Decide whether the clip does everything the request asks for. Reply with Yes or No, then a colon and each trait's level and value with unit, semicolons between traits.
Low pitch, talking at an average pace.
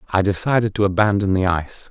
Yes: low, 100 Hz; average, 190 wpm